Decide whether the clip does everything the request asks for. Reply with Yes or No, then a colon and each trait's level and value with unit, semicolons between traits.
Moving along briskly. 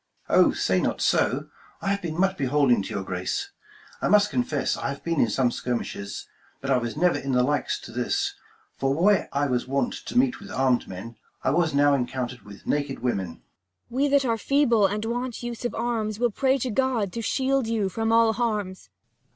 Yes: fast, 215 wpm